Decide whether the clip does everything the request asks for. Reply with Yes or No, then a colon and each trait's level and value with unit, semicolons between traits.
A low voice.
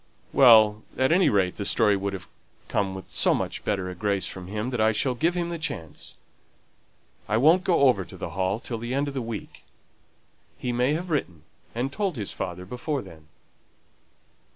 Yes: low, 110 Hz